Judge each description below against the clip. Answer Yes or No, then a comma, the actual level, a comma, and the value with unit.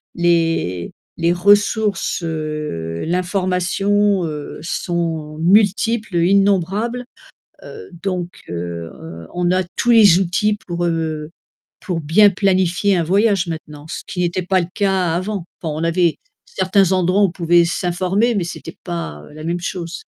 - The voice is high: No, medium, 175 Hz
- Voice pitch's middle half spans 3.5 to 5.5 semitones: No, average, 3.0 semitones